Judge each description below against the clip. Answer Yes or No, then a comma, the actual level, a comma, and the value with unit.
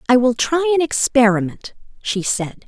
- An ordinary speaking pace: Yes, average, 155 wpm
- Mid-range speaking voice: No, very high, 250 Hz